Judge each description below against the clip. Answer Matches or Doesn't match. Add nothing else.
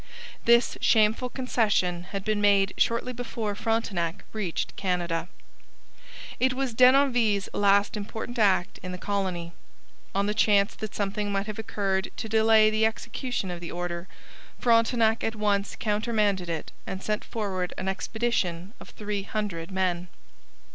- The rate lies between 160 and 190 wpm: Doesn't match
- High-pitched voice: Matches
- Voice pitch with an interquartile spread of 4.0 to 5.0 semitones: Doesn't match